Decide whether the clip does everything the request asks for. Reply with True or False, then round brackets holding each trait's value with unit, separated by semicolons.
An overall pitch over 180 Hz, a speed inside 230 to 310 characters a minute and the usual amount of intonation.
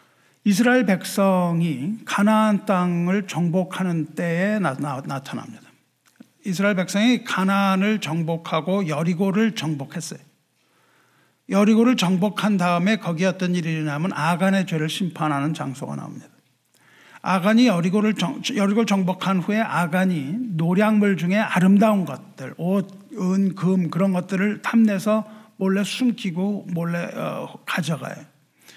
True (190 Hz; 290 characters per minute; 3.3 semitones)